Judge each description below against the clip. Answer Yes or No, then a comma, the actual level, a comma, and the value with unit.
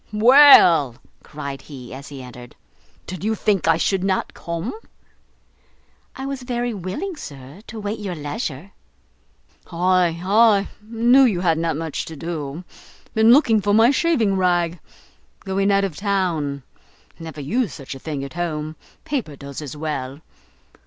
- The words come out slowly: No, average, 150 wpm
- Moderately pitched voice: Yes, medium, 175 Hz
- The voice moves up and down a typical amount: No, wide, 6.2 semitones